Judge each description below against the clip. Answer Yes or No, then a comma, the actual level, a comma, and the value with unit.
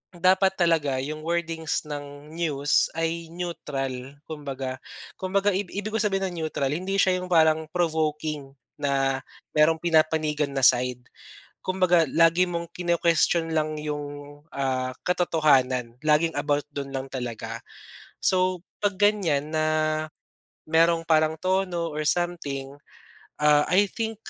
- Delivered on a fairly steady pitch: No, average, 3.4 semitones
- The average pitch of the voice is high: No, medium, 155 Hz